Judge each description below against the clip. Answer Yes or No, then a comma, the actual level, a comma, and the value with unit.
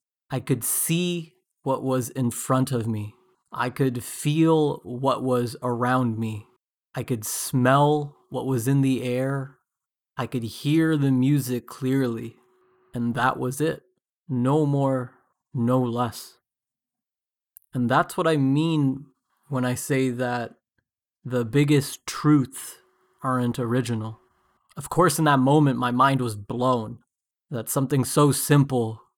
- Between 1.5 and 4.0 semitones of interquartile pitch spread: Yes, average, 2.7 semitones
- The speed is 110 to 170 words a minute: Yes, slow, 135 wpm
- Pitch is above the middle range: No, low, 130 Hz